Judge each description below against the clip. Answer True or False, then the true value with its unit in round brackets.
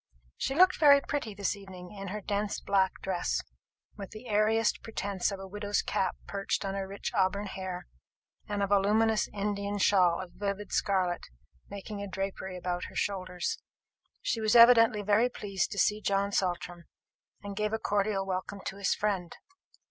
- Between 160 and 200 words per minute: True (170 wpm)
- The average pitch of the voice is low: False (200 Hz)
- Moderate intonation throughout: False (1.8 semitones)